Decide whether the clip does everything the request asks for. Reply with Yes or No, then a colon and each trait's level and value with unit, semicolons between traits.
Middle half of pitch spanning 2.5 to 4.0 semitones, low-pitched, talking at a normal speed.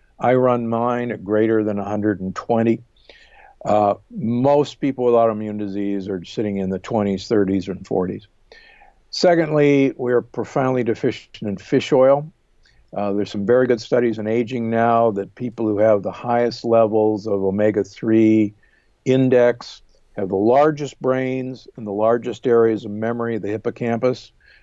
Yes: average, 2.8 semitones; low, 115 Hz; average, 145 wpm